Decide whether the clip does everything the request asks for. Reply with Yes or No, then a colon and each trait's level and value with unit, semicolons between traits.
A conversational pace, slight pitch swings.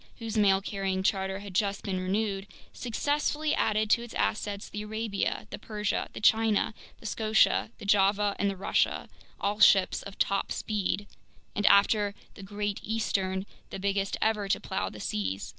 Yes: average, 165 wpm; narrow, 1.8 semitones